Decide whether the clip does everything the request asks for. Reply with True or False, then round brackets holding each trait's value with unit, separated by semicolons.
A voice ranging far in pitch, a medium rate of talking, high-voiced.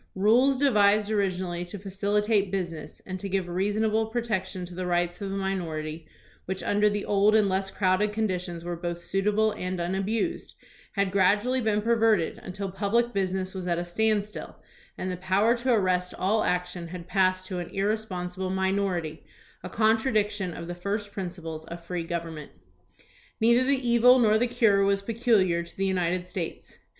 False (3.1 semitones; 165 wpm; 195 Hz)